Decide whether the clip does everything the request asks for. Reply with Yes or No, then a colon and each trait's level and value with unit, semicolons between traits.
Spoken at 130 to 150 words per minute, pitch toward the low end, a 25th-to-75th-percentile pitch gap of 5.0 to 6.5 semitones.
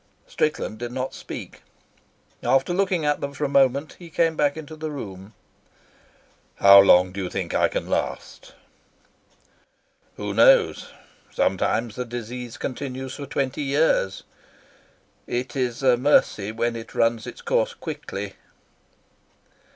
No: slow, 135 wpm; low, 130 Hz; average, 4.3 semitones